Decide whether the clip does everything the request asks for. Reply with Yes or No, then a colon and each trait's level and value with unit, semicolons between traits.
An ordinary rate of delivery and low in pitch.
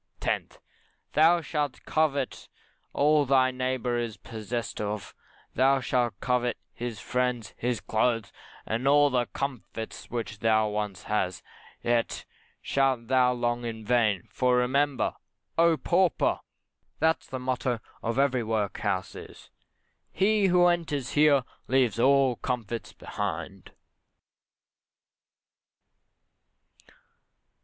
No: slow, 110 wpm; low, 125 Hz